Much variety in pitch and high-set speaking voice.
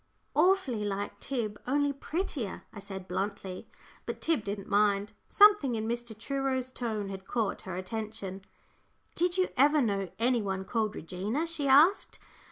Yes: wide, 5.7 semitones; high, 220 Hz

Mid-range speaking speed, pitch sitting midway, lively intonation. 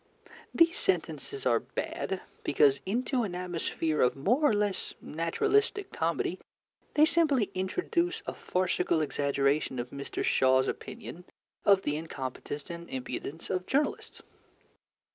No: slow, 125 wpm; medium, 180 Hz; wide, 8.9 semitones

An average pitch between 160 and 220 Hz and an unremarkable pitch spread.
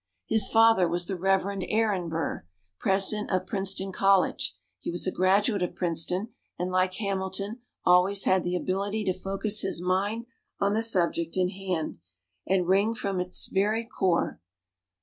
No: high, 190 Hz; narrow, 2.0 semitones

